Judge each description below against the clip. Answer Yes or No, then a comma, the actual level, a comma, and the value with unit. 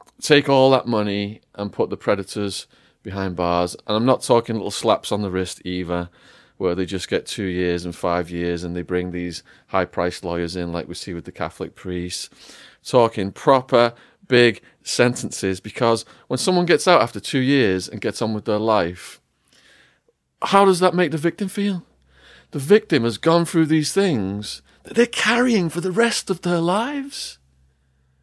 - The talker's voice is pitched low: Yes, low, 105 Hz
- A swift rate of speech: No, average, 180 wpm